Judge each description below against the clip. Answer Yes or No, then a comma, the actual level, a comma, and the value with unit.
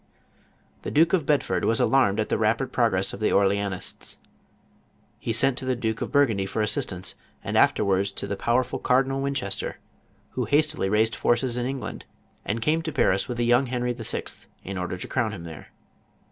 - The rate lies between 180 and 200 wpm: Yes, average, 195 wpm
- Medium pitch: No, low, 115 Hz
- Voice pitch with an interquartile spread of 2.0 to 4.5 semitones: No, average, 4.9 semitones